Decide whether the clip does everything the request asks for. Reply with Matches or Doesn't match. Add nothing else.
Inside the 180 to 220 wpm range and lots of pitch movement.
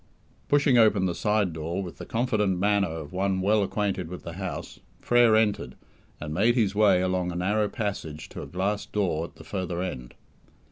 Doesn't match